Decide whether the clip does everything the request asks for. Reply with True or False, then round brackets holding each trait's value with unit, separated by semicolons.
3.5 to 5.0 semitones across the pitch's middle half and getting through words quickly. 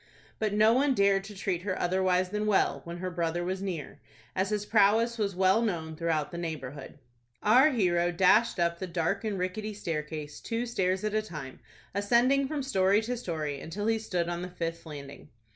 False (4.0 semitones; 195 wpm)